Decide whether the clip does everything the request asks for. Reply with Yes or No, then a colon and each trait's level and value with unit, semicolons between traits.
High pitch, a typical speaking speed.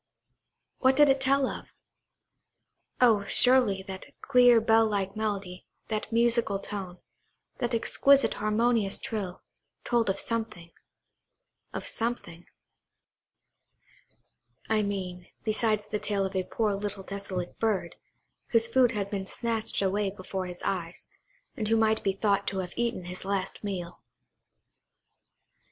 No: high, 210 Hz; slow, 125 wpm